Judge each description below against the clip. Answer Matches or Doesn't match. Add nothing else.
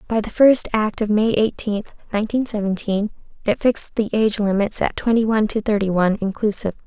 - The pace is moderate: Matches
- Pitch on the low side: Doesn't match